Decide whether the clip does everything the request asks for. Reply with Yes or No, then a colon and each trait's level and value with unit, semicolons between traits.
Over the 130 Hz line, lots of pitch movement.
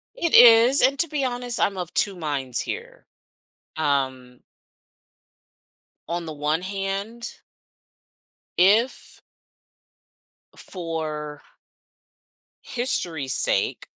Yes: medium, 185 Hz; wide, 8.2 semitones